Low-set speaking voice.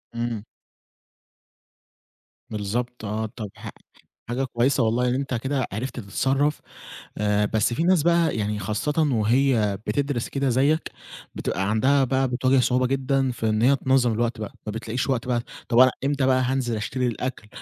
Yes: low, 125 Hz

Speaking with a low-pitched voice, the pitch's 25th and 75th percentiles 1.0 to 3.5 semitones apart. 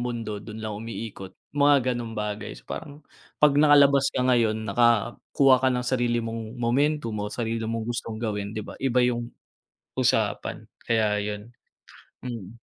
Yes: low, 115 Hz; narrow, 2.6 semitones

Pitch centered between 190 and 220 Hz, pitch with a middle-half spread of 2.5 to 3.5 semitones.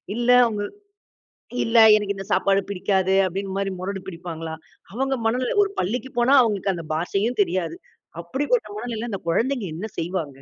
No: high, 200 Hz; average, 4.4 semitones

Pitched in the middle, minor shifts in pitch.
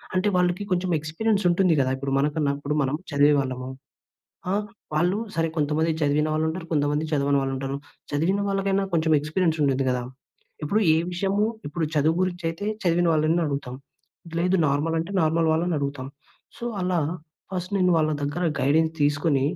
No: medium, 160 Hz; average, 3.7 semitones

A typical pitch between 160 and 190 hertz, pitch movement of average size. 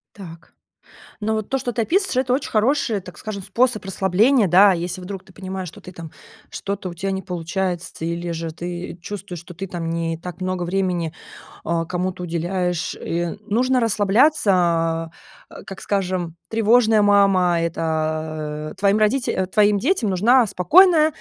Yes: medium, 185 Hz; average, 3.6 semitones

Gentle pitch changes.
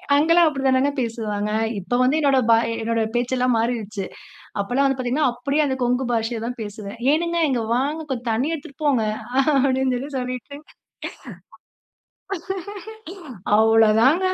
No: average, 3.5 semitones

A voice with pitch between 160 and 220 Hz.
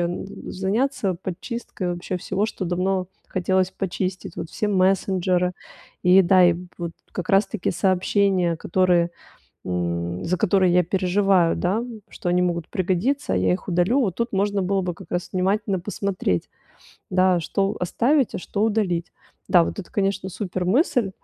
Yes: medium, 185 Hz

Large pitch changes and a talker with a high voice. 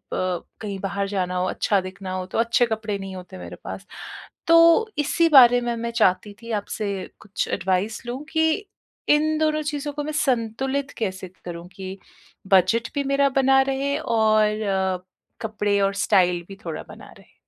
Yes: wide, 6.1 semitones; high, 215 Hz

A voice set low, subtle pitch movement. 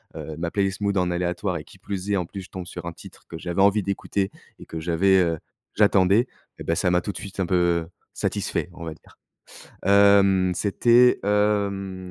Yes: very low, 95 Hz; narrow, 2.3 semitones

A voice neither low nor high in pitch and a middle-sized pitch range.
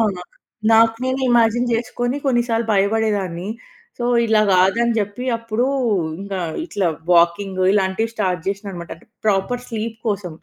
No: high, 215 Hz; average, 3.4 semitones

